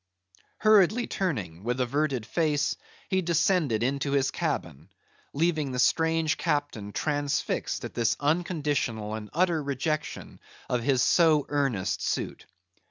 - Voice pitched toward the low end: No, medium, 145 Hz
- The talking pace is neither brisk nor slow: No, slow, 120 wpm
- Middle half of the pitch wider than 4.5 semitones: Yes, average, 4.9 semitones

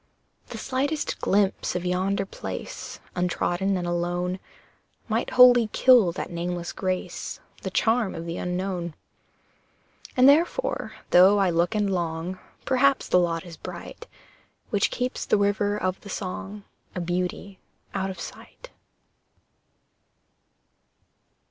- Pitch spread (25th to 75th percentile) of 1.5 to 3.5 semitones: Yes, average, 3.1 semitones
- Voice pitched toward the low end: No, high, 190 Hz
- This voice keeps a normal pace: No, slow, 125 wpm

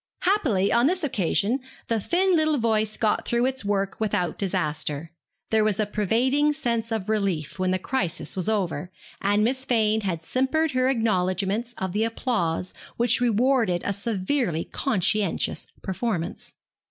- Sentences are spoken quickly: No, average, 150 wpm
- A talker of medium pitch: No, high, 215 Hz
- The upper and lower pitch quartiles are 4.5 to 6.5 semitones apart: Yes, average, 4.9 semitones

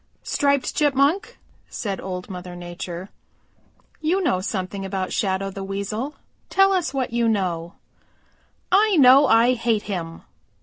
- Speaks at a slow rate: Yes, slow, 130 wpm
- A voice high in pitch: Yes, high, 210 Hz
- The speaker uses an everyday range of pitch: No, wide, 6.9 semitones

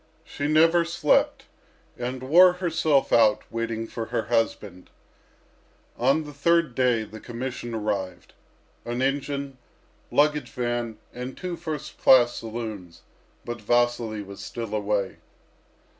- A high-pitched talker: No, low, 120 Hz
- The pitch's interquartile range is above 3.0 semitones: Yes, average, 4.5 semitones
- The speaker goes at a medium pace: No, slow, 120 wpm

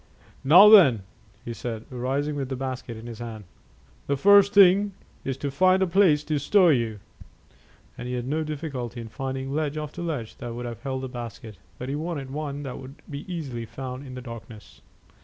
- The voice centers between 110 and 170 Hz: Yes, low, 135 Hz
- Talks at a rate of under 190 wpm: No, average, 195 wpm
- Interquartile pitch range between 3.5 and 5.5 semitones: Yes, average, 4.1 semitones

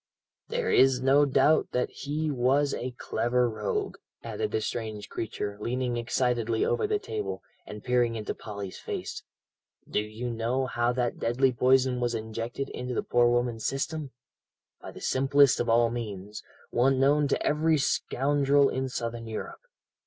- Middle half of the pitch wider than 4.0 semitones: No, average, 2.9 semitones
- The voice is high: No, low, 125 Hz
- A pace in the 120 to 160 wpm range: Yes, average, 155 wpm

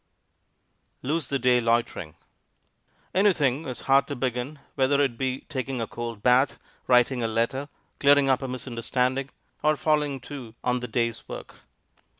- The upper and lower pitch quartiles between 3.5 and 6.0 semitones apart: No, narrow, 2.5 semitones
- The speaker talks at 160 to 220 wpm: No, average, 150 wpm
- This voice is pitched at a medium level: No, low, 130 Hz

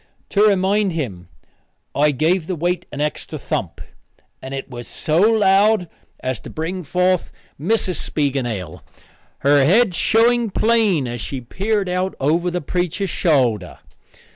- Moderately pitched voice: Yes, medium, 175 Hz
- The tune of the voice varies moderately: No, wide, 5.7 semitones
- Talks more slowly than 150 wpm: Yes, average, 140 wpm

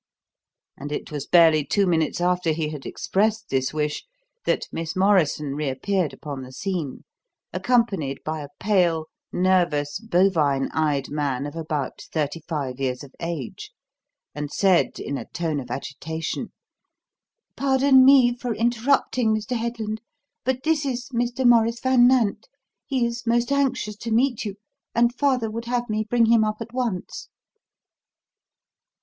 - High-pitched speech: Yes, high, 195 Hz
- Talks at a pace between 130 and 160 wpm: Yes, average, 145 wpm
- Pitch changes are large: Yes, wide, 7.8 semitones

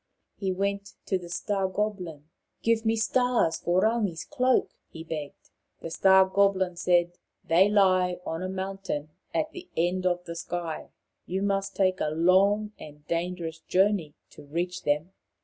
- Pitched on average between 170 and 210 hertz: Yes, medium, 185 Hz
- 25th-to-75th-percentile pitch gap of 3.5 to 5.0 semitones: No, average, 2.9 semitones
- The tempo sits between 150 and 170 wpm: Yes, average, 165 wpm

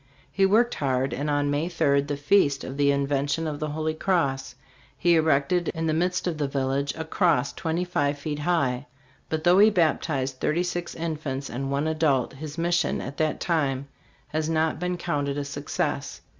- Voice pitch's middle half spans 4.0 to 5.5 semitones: No, average, 3.1 semitones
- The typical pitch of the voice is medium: Yes, medium, 150 Hz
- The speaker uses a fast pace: No, average, 185 wpm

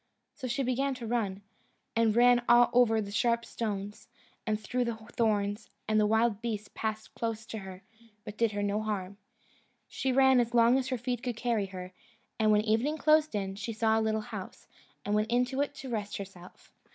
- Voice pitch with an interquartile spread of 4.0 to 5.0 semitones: No, average, 2.7 semitones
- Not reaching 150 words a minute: No, average, 195 wpm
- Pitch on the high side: Yes, high, 220 Hz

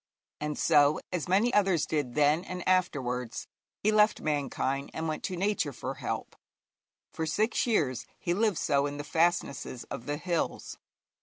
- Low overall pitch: No, medium, 160 Hz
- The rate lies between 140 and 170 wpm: Yes, average, 160 wpm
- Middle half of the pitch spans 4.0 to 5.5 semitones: Yes, average, 4.4 semitones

